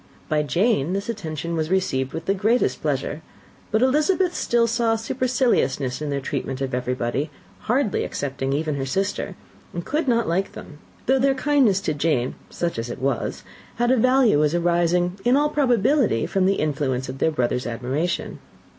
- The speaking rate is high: No, average, 170 wpm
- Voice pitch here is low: No, medium, 175 Hz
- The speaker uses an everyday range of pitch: No, wide, 9.0 semitones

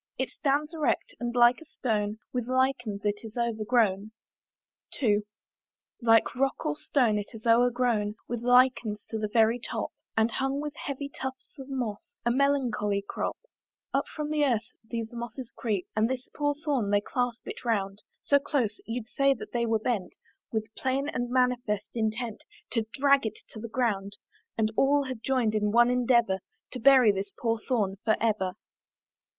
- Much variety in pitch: No, average, 3.3 semitones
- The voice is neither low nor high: No, high, 235 Hz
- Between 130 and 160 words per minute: No, average, 170 wpm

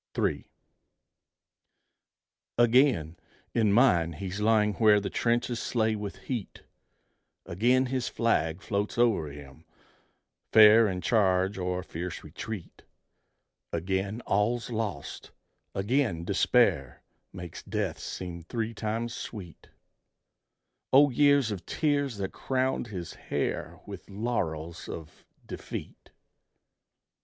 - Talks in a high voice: No, low, 105 Hz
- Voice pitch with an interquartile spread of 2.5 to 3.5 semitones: No, average, 4.8 semitones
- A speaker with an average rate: No, slow, 105 wpm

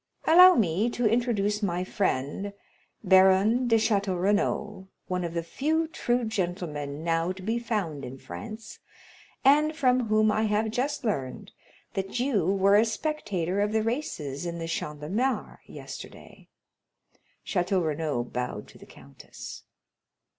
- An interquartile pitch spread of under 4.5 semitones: No, average, 5.1 semitones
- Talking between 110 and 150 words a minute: Yes, average, 145 wpm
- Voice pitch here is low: No, high, 200 Hz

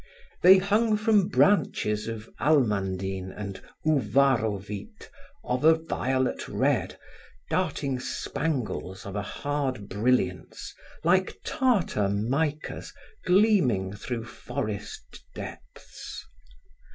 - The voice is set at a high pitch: No, low, 130 Hz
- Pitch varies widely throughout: Yes, wide, 7.8 semitones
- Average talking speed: No, slow, 90 wpm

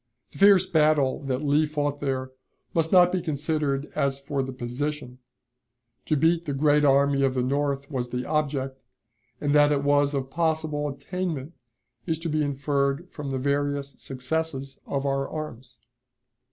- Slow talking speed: No, average, 160 wpm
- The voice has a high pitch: No, medium, 145 Hz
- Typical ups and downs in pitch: No, narrow, 2.1 semitones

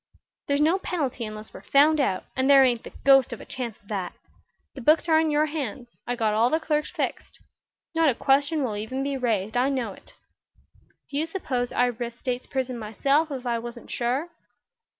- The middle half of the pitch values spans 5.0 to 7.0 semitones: No, average, 3.8 semitones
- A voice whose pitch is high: Yes, very high, 260 Hz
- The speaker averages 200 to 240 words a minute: Yes, fast, 205 wpm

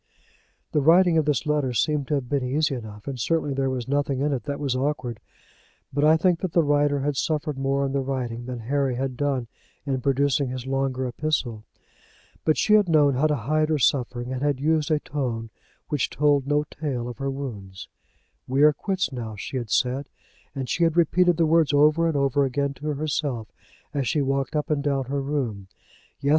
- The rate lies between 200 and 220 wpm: Yes, fast, 205 wpm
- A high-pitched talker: No, medium, 140 Hz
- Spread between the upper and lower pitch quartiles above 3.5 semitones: No, average, 2.7 semitones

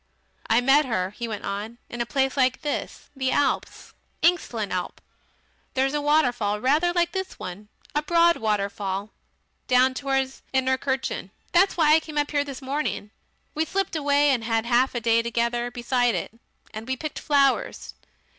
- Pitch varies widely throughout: No, average, 4.2 semitones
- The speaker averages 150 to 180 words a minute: Yes, average, 165 wpm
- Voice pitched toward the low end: No, very high, 260 Hz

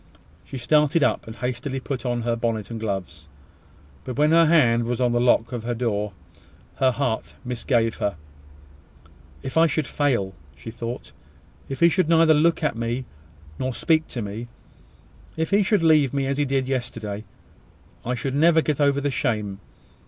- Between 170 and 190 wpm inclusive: Yes, average, 175 wpm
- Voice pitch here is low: Yes, low, 125 Hz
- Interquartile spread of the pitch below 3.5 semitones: No, average, 4.3 semitones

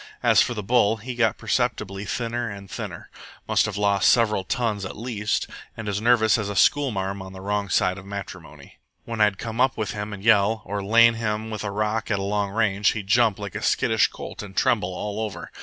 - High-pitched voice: No, low, 105 Hz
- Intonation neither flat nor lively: No, narrow, 2.3 semitones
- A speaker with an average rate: No, fast, 215 wpm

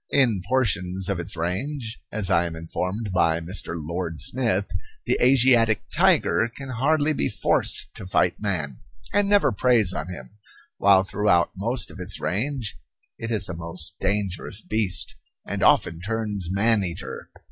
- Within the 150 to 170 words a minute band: Yes, average, 155 wpm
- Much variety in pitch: No, average, 4.4 semitones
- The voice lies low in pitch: Yes, low, 100 Hz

